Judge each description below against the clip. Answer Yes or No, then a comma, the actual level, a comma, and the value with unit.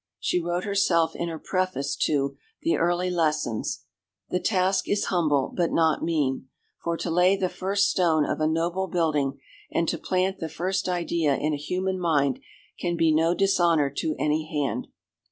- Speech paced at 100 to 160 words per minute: No, average, 170 wpm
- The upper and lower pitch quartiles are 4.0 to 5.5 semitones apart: No, average, 2.9 semitones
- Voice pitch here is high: No, medium, 170 Hz